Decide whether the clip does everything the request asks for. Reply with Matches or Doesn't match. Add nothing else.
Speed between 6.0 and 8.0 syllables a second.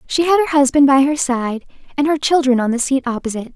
Matches